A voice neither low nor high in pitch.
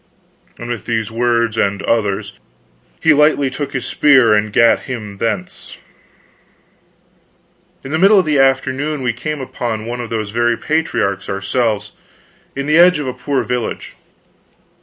No: low, 120 Hz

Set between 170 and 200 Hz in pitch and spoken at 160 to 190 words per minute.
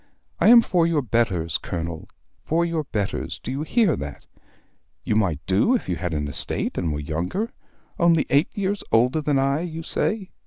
No: medium, 140 Hz; average, 185 wpm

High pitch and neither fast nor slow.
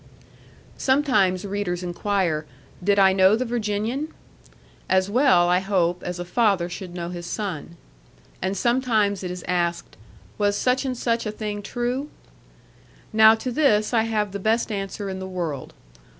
Yes: high, 200 Hz; average, 155 wpm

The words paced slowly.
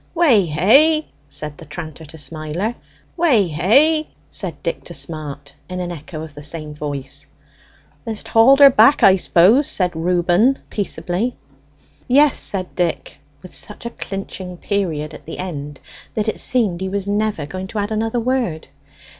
No: average, 160 wpm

